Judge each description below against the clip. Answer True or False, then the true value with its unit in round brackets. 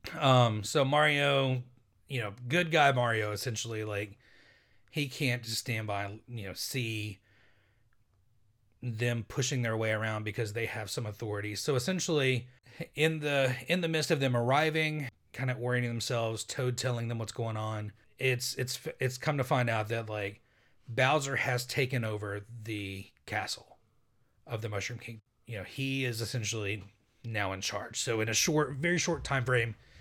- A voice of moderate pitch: False (120 Hz)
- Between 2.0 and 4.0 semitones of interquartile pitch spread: True (3.5 semitones)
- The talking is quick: False (165 wpm)